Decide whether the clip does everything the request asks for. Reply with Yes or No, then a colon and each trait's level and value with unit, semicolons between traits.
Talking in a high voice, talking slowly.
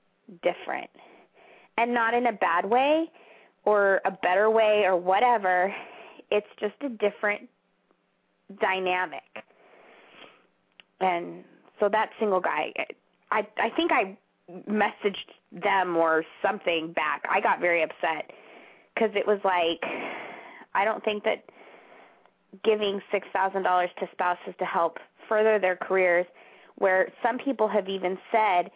Yes: high, 195 Hz; slow, 125 wpm